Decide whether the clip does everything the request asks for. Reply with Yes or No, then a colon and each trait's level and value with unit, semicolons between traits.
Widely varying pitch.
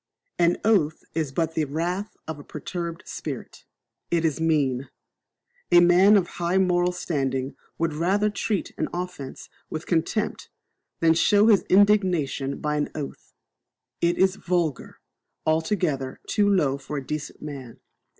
No: average, 3.6 semitones